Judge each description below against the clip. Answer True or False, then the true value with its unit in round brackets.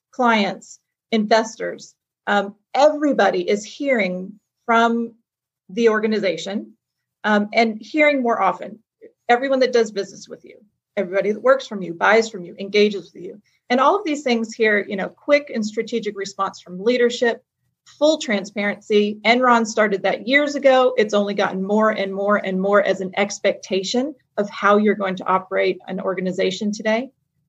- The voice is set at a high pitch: True (210 Hz)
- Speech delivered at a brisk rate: False (155 wpm)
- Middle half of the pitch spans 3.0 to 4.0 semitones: True (3.5 semitones)